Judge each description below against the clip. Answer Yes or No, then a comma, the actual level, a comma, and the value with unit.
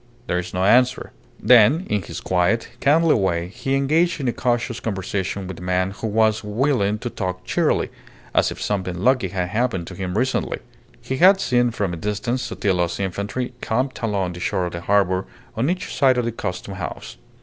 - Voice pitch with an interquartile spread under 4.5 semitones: No, average, 5.2 semitones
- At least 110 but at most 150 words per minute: No, average, 195 wpm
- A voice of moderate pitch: No, low, 105 Hz